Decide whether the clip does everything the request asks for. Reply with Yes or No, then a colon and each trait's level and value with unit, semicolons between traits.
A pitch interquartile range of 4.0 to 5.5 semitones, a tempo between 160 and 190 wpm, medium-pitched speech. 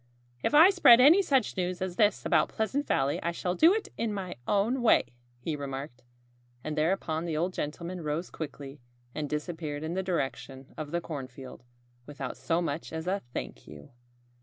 Yes: average, 5.1 semitones; average, 180 wpm; medium, 165 Hz